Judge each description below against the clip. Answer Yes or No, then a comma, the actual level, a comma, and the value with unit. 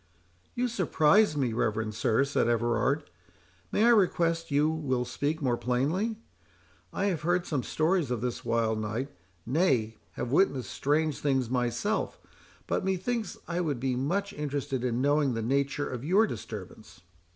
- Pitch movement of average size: No, wide, 5.9 semitones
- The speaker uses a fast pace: No, average, 150 wpm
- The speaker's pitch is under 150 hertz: Yes, medium, 140 Hz